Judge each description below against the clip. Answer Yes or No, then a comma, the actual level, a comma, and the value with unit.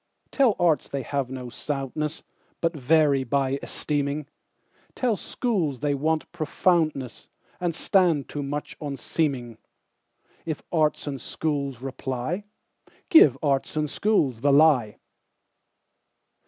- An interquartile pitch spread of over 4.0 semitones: No, average, 3.0 semitones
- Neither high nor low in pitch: Yes, medium, 145 Hz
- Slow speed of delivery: Yes, slow, 100 wpm